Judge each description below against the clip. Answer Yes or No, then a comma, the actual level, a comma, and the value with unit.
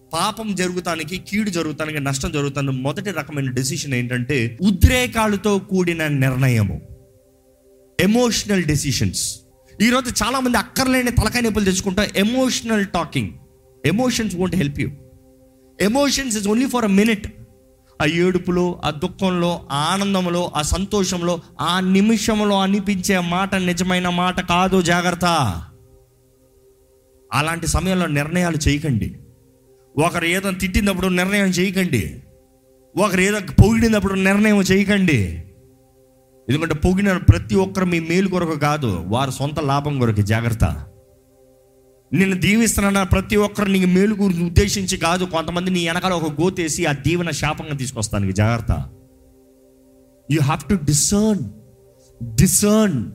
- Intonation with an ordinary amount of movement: No, wide, 6.8 semitones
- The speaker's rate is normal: Yes, average, 110 wpm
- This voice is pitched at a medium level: Yes, medium, 170 Hz